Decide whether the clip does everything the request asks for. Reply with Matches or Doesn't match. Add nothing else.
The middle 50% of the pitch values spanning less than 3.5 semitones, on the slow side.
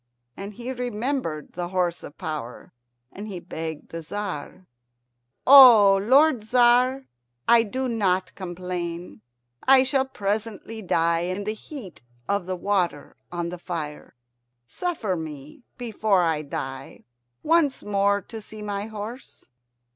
Doesn't match